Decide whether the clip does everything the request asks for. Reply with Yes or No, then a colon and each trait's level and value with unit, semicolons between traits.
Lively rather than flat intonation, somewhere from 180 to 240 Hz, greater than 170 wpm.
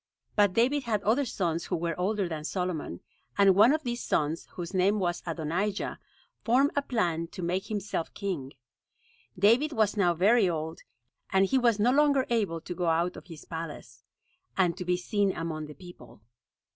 No: average, 4.5 semitones; medium, 185 Hz; average, 180 wpm